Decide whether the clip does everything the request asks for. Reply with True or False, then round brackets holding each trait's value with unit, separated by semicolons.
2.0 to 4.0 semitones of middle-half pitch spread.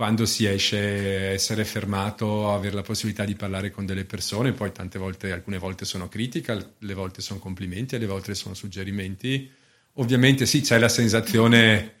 True (2.7 semitones)